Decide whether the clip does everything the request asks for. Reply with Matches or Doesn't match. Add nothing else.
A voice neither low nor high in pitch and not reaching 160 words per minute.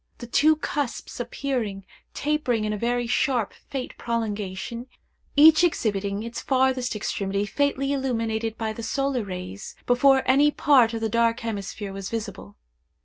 Doesn't match